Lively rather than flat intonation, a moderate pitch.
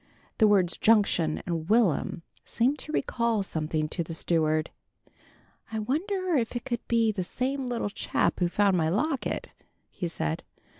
No: wide, 6.2 semitones; high, 210 Hz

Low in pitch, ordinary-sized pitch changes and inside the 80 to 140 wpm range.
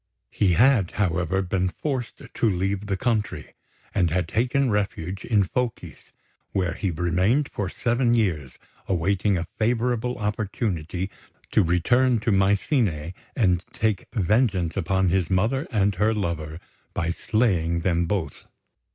Yes: low, 100 Hz; average, 4.2 semitones; slow, 135 wpm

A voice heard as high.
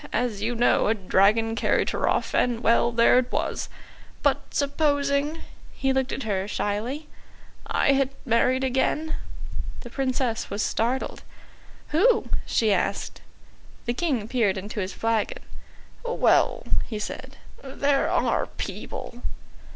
Yes: high, 245 Hz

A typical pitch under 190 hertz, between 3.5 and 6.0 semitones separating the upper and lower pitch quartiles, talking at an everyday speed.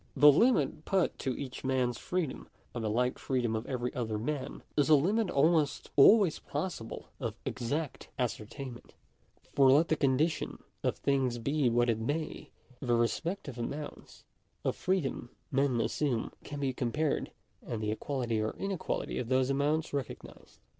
Yes: low, 135 Hz; average, 4.0 semitones; average, 155 wpm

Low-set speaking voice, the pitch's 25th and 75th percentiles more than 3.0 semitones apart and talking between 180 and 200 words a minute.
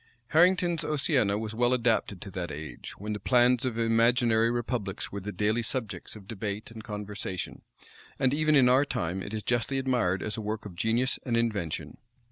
Yes: low, 115 Hz; average, 3.4 semitones; average, 185 wpm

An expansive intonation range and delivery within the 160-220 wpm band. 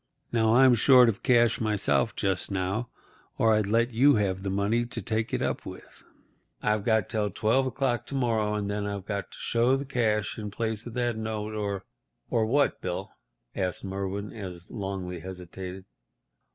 No: average, 3.1 semitones; average, 180 wpm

